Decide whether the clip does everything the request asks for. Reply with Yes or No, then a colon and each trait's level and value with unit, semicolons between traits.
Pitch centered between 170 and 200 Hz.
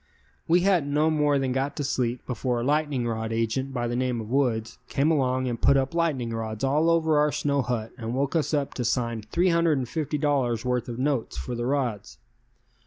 No: low, 130 Hz